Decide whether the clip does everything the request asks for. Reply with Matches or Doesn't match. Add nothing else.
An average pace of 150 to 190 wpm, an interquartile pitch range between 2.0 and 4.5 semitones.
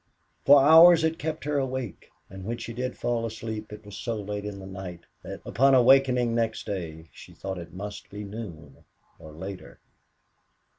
Doesn't match